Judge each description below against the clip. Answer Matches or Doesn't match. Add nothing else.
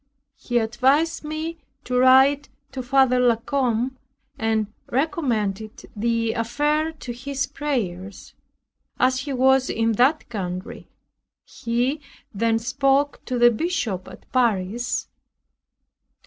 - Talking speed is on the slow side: Matches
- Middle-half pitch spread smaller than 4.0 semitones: Matches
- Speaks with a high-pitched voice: Matches